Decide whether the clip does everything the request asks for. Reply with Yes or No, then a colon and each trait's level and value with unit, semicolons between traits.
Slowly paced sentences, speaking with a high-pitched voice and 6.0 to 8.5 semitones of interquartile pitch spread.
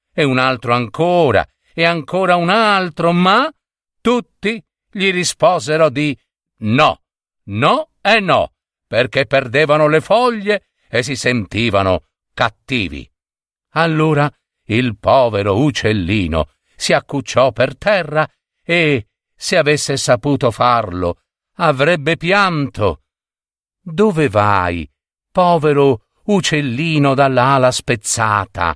No: slow, 95 wpm; medium, 140 Hz; wide, 6.7 semitones